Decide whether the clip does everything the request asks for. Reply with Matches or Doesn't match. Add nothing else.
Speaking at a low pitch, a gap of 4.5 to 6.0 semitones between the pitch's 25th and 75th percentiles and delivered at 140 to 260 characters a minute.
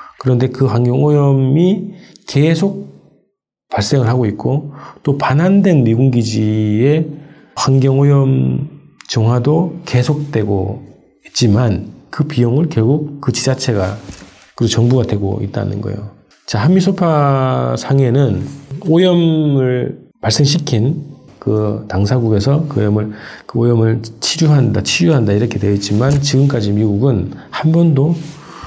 Matches